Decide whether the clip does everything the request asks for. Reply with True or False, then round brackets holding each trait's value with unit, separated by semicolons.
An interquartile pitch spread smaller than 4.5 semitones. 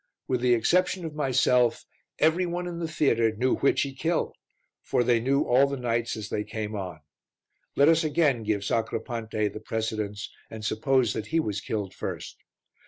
False (4.8 semitones)